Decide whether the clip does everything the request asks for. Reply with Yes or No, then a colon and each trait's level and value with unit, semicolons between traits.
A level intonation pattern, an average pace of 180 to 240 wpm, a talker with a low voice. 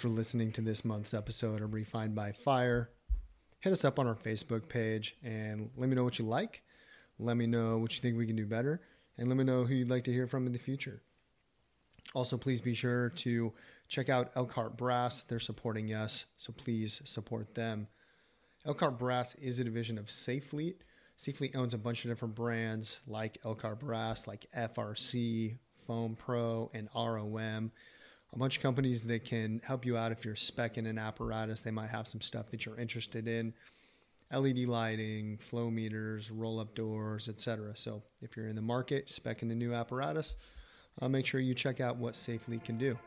Yes: narrow, 2.2 semitones; average, 190 wpm; low, 115 Hz